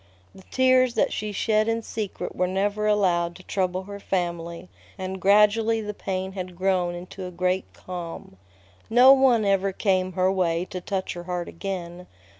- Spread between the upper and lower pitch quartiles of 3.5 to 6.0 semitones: No, narrow, 2.5 semitones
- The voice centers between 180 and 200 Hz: Yes, high, 190 Hz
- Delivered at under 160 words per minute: No, average, 170 wpm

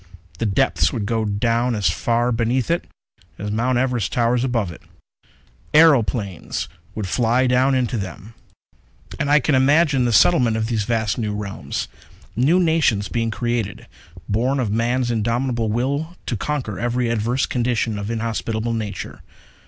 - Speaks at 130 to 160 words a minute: Yes, average, 150 wpm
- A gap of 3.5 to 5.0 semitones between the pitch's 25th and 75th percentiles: No, narrow, 2.6 semitones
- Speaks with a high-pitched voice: No, low, 120 Hz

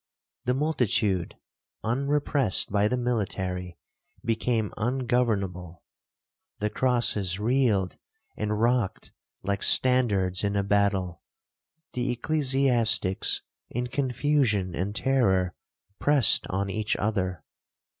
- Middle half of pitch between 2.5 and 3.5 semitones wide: No, average, 4.7 semitones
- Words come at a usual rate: No, slow, 95 wpm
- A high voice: No, low, 110 Hz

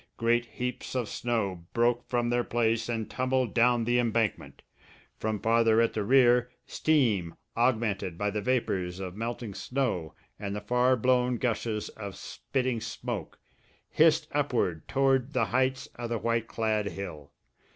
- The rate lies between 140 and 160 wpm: Yes, average, 150 wpm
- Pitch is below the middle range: Yes, low, 115 Hz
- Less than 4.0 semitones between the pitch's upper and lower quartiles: Yes, average, 2.8 semitones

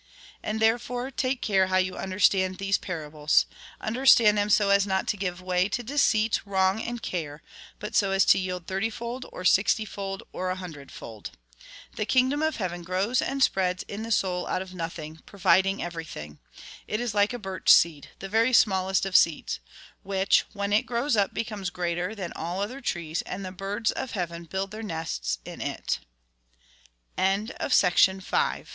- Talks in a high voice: Yes, high, 195 Hz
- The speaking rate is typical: Yes, average, 160 wpm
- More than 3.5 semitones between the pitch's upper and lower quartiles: No, average, 3.2 semitones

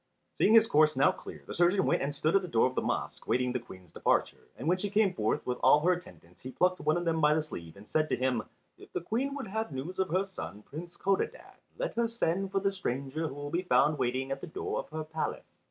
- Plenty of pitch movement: Yes, wide, 6.0 semitones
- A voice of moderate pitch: Yes, medium, 160 Hz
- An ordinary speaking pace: No, fast, 265 wpm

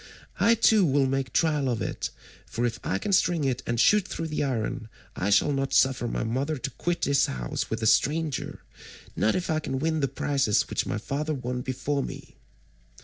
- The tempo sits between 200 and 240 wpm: Yes, fast, 205 wpm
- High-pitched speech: No, low, 135 Hz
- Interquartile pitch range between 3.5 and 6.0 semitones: Yes, average, 4.3 semitones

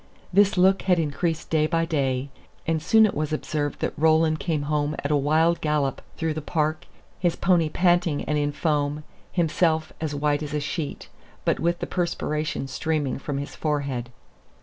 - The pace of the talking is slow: No, average, 175 wpm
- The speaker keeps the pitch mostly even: Yes, narrow, 2.2 semitones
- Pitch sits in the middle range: Yes, medium, 155 Hz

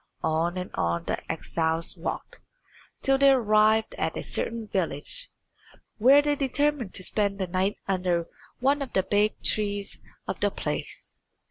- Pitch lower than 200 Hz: No, high, 205 Hz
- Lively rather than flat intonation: Yes, wide, 6.3 semitones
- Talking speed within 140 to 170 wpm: Yes, average, 150 wpm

